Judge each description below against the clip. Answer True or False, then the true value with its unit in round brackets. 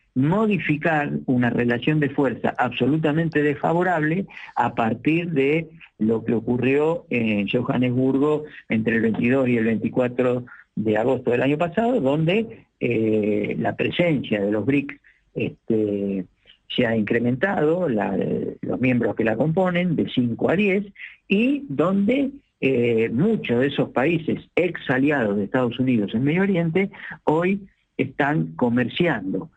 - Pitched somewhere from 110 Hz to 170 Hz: True (135 Hz)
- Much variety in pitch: True (5.9 semitones)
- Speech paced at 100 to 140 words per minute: True (130 wpm)